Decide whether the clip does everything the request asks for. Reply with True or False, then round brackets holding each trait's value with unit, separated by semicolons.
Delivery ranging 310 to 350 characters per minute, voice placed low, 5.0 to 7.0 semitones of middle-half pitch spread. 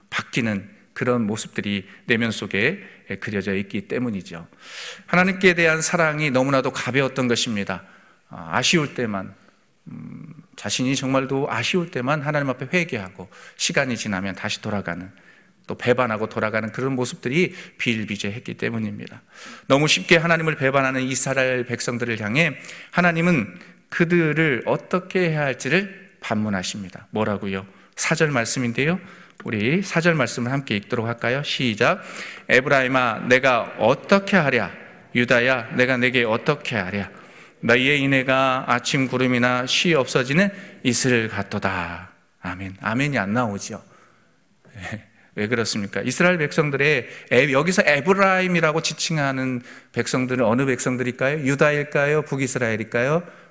True (320 characters per minute; 130 Hz; 5.6 semitones)